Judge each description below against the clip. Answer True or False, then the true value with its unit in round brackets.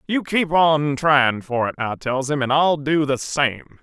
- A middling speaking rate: False (220 wpm)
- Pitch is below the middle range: False (145 Hz)